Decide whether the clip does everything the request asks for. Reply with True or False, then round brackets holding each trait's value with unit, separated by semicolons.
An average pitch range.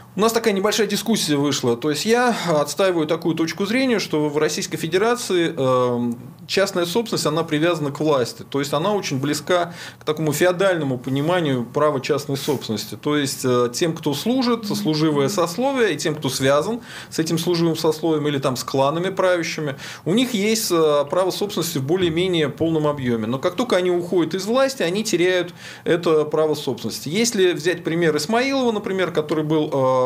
True (4.3 semitones)